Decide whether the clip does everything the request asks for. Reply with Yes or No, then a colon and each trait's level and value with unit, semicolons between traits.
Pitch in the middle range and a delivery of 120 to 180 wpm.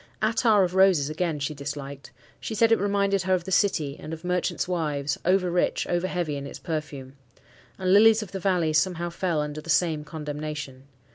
No: medium, 170 Hz; average, 195 wpm